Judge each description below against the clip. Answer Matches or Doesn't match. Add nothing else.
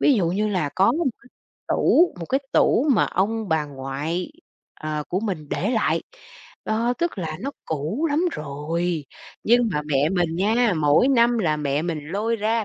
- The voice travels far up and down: Matches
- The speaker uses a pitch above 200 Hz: Doesn't match